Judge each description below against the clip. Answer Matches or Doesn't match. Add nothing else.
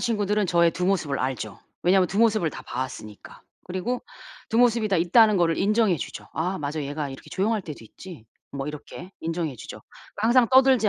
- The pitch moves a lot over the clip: Matches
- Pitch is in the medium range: Matches